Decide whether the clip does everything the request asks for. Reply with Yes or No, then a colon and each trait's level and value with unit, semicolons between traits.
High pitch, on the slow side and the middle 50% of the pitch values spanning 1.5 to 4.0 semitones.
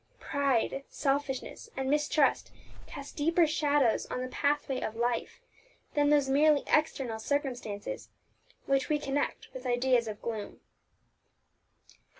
Yes: very high, 275 Hz; slow, 120 wpm; average, 2.8 semitones